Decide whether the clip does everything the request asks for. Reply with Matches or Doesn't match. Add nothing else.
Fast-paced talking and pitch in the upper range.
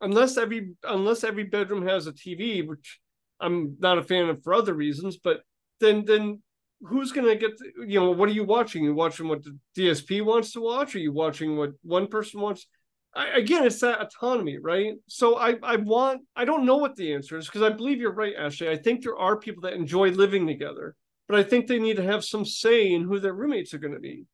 Matches